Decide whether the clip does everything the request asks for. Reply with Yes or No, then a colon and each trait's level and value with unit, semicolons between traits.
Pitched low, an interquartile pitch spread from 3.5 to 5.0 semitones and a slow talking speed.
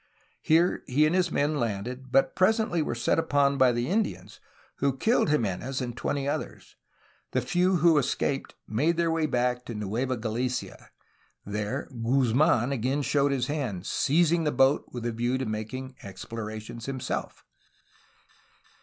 No: low, 130 Hz; average, 4.3 semitones; average, 155 wpm